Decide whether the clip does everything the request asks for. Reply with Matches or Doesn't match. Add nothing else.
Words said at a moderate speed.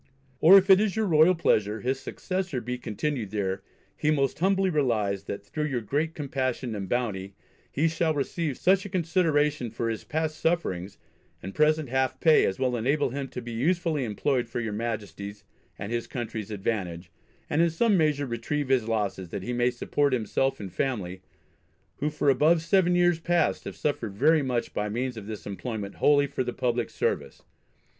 Matches